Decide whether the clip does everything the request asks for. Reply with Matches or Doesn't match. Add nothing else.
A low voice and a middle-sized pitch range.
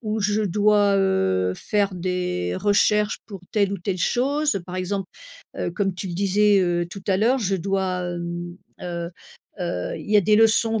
Doesn't match